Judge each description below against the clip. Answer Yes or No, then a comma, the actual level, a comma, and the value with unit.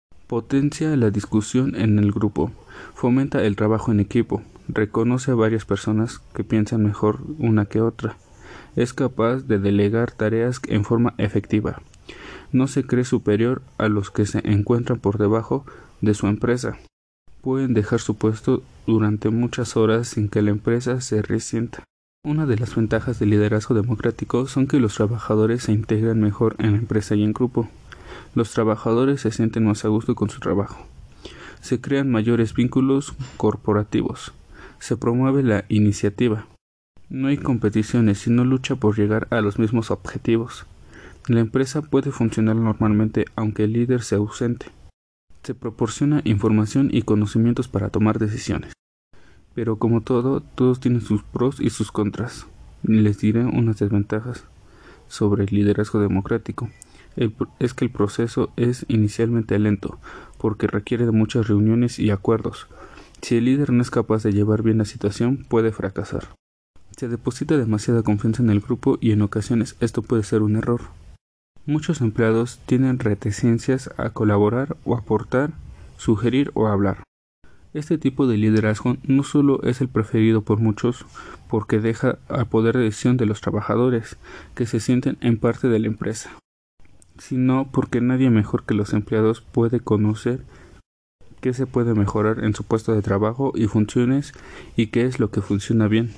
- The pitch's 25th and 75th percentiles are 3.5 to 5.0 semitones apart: No, narrow, 2.6 semitones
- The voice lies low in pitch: Yes, low, 115 Hz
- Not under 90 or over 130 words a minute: No, average, 155 wpm